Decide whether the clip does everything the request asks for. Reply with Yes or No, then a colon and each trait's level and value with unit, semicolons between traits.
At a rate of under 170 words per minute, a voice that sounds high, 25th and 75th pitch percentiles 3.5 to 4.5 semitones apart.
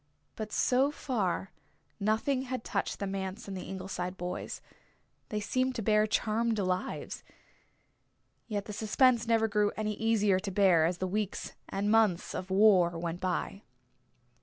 No: average, 150 wpm; high, 205 Hz; average, 3.0 semitones